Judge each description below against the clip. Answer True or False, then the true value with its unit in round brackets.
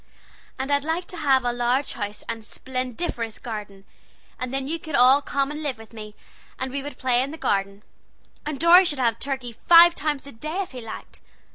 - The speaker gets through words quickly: True (215 wpm)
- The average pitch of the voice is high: True (265 Hz)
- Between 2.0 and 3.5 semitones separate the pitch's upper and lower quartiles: False (4.3 semitones)